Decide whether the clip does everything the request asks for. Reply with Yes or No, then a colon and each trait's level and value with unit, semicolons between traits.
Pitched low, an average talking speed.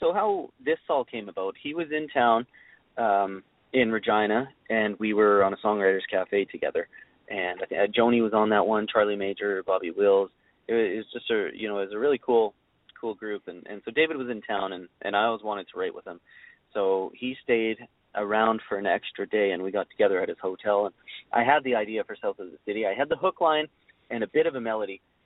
No: low, 110 Hz; fast, 230 wpm